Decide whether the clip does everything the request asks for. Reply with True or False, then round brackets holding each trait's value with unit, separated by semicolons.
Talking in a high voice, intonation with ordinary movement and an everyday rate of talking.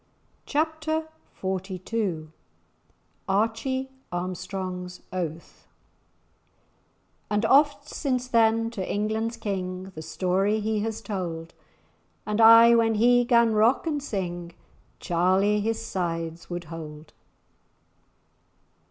False (210 Hz; 4.1 semitones; 95 wpm)